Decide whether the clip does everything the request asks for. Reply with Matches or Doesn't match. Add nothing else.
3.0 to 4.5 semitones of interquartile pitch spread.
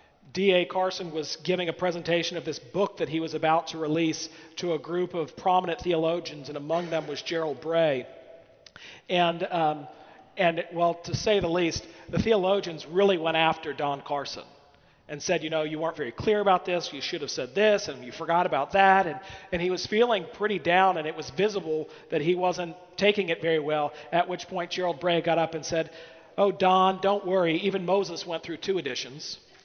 Doesn't match